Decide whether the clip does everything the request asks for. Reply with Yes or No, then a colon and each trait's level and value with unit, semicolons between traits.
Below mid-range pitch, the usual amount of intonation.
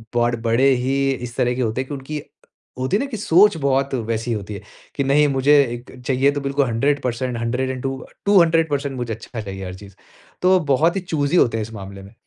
Yes: low, 130 Hz; average, 3.8 semitones